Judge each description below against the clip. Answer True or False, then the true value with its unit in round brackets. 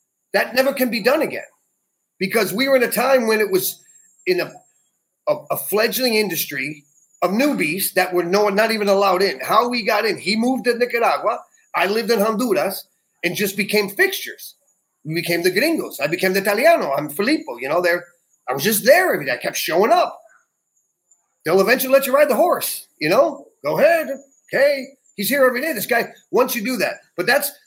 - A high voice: True (225 Hz)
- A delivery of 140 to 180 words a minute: False (205 wpm)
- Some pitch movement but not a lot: False (6.3 semitones)